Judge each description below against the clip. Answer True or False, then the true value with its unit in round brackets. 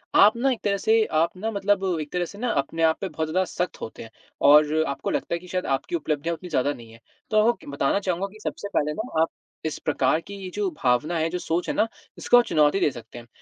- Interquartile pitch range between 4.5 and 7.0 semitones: True (5.1 semitones)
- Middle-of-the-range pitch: True (170 Hz)